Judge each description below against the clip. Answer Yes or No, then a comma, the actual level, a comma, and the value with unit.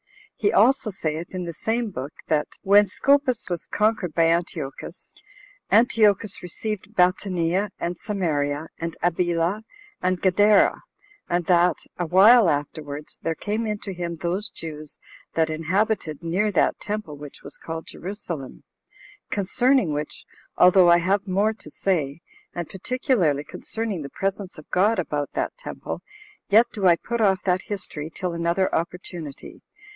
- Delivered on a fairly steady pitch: No, average, 4.1 semitones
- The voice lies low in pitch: No, medium, 180 Hz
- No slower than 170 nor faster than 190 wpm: No, average, 145 wpm